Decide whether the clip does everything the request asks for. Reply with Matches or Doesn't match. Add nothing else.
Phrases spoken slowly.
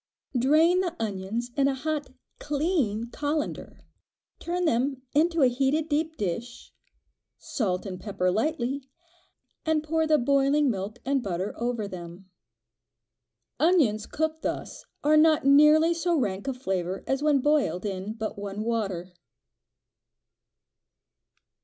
Matches